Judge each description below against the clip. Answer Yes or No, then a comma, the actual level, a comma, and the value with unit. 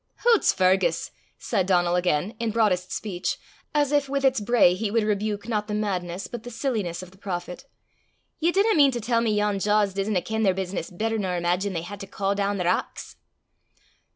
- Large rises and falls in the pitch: No, average, 3.7 semitones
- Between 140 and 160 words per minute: No, fast, 205 wpm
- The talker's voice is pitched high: Yes, high, 205 Hz